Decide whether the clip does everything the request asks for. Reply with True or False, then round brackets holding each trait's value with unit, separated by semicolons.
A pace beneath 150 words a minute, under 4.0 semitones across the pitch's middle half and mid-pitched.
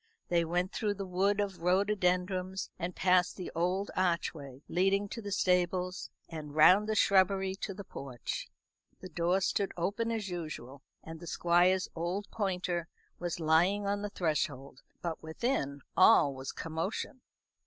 False (155 wpm; 2.9 semitones; 180 Hz)